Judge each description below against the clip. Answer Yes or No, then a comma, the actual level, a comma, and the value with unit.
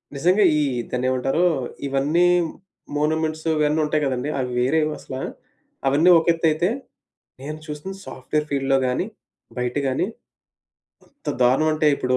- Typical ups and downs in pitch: Yes, average, 3.1 semitones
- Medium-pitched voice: Yes, medium, 150 Hz